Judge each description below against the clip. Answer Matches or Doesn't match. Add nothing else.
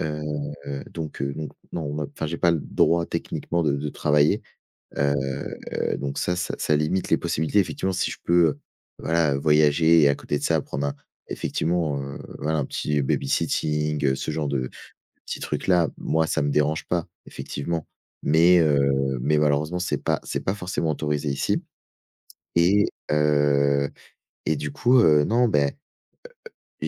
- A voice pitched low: Matches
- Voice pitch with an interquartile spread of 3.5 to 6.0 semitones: Doesn't match